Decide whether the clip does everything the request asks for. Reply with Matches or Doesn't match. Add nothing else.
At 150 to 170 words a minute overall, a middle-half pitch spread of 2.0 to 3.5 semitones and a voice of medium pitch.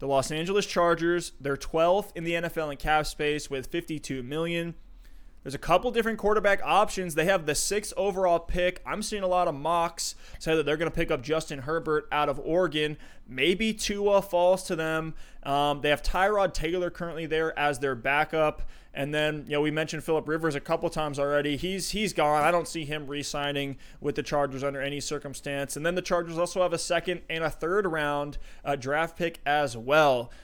Doesn't match